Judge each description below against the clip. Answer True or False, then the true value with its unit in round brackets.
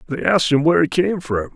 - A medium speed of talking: False (270 wpm)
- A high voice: False (145 Hz)